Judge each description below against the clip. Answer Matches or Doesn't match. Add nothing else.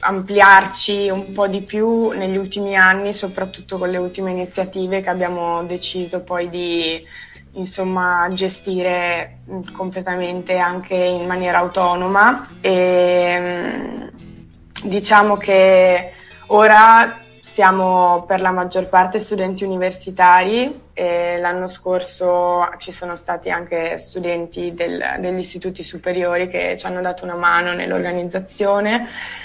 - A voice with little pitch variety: Matches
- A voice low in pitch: Doesn't match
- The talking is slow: Matches